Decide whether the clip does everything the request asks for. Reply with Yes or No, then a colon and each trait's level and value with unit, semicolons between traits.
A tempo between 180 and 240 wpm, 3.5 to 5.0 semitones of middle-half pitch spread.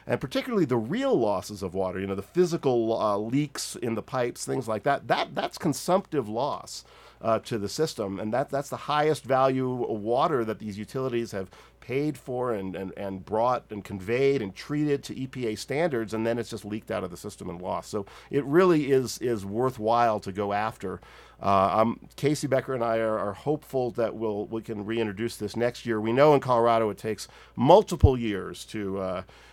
Yes: average, 200 wpm; average, 4.2 semitones